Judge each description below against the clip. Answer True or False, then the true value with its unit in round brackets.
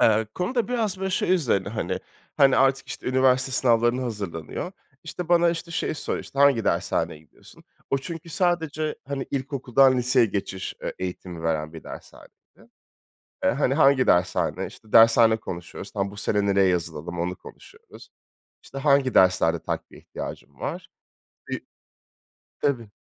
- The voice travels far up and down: True (6.8 semitones)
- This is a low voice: True (125 Hz)